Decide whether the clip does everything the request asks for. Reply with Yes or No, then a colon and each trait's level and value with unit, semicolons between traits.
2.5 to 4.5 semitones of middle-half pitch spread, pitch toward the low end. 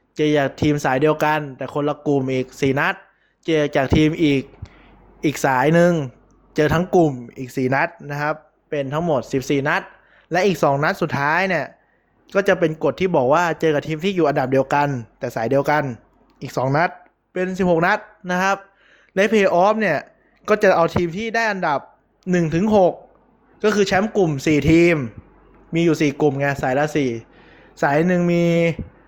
No: average, 4.1 semitones; medium, 155 Hz